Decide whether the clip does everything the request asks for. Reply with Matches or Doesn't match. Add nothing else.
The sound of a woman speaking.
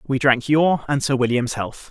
Doesn't match